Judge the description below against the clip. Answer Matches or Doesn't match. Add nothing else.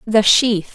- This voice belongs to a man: Doesn't match